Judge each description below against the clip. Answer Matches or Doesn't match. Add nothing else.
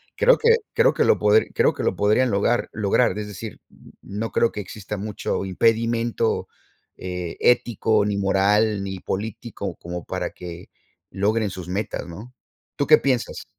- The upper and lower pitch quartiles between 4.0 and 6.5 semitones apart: Doesn't match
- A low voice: Matches